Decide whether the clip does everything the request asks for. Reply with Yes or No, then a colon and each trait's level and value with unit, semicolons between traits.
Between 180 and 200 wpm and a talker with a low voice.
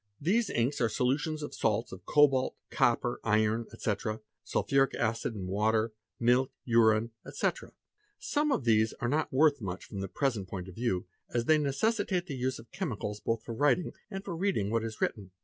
Yes: average, 185 wpm; low, 120 Hz